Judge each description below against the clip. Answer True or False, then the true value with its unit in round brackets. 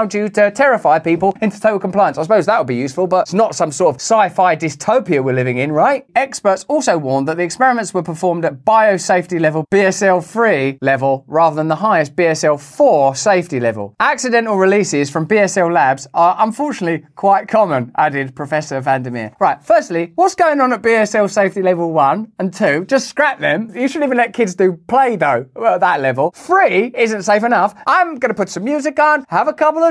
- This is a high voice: True (195 Hz)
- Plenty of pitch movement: True (6.4 semitones)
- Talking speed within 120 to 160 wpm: False (205 wpm)